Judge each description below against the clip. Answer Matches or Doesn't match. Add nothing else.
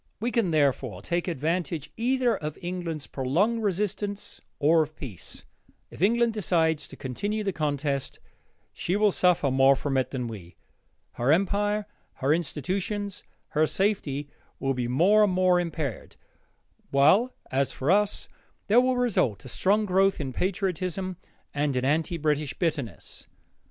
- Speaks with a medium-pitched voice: Matches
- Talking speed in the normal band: Matches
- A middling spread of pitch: Doesn't match